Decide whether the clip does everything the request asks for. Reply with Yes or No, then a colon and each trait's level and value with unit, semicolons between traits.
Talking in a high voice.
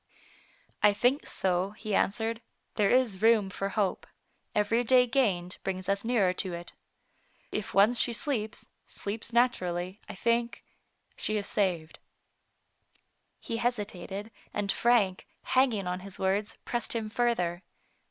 Yes: high, 210 Hz